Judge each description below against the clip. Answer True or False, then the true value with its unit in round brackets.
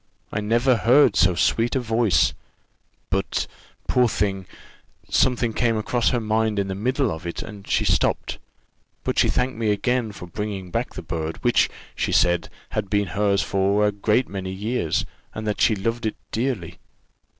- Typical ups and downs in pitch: True (3.3 semitones)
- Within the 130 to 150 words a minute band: False (170 wpm)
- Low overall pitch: True (105 Hz)